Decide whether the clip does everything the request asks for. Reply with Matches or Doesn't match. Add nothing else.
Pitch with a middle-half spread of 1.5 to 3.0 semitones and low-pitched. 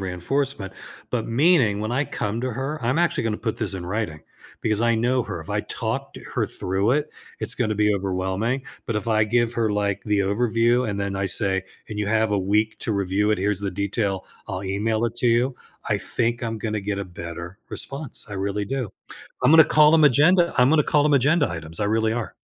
Doesn't match